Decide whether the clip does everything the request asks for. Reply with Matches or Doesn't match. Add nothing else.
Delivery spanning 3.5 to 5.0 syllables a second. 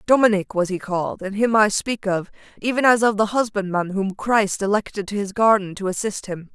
Doesn't match